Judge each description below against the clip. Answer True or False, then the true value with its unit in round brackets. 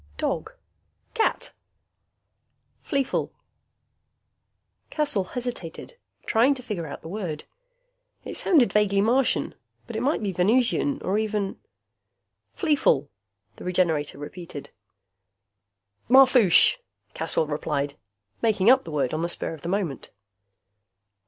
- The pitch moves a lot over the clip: True (7.5 semitones)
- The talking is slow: True (110 wpm)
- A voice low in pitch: False (205 Hz)